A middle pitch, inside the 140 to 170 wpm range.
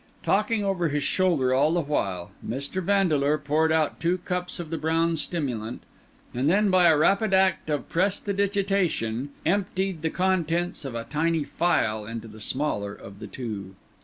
Yes: medium, 160 Hz; average, 160 wpm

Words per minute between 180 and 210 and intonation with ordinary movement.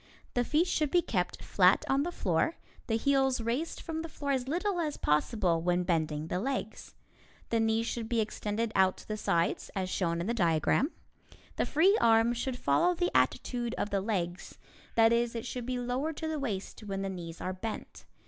No: average, 195 wpm; wide, 6.5 semitones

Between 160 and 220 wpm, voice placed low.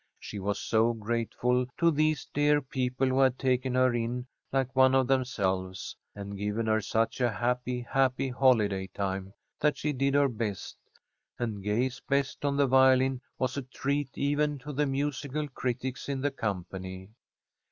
Yes: average, 165 wpm; low, 130 Hz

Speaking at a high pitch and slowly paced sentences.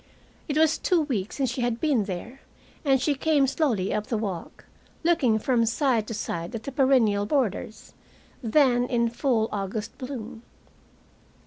No: high, 240 Hz; average, 155 wpm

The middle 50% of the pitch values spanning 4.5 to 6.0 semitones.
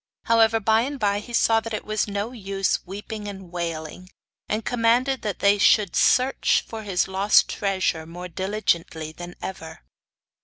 No: average, 3.7 semitones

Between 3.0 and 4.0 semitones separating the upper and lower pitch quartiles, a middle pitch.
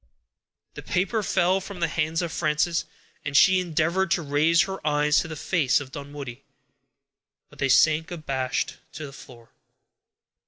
Yes: average, 3.3 semitones; medium, 155 Hz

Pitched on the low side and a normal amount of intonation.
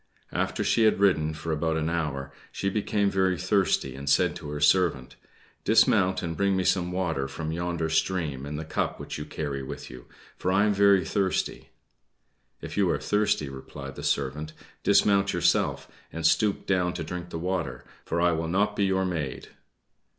Yes: very low, 85 Hz; average, 3.9 semitones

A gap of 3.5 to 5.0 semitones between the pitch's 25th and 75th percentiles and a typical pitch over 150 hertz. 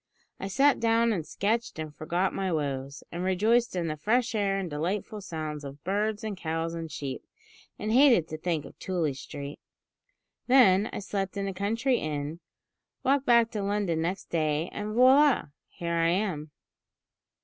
No: wide, 5.4 semitones; high, 190 Hz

